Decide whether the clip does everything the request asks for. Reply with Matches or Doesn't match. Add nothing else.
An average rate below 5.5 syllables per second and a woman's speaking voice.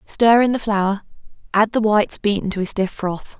Matches